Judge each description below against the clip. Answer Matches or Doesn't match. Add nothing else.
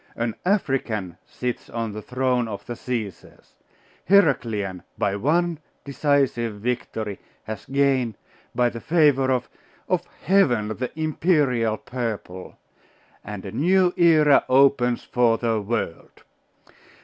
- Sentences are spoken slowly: Matches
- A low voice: Matches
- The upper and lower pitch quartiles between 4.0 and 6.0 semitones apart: Matches